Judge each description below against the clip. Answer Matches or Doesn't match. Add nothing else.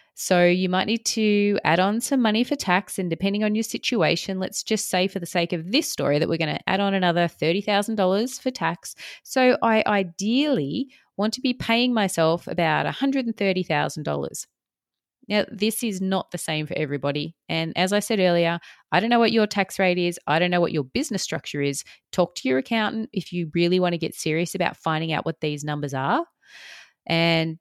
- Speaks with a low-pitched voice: Doesn't match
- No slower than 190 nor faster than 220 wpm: Matches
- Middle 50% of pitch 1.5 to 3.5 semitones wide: Doesn't match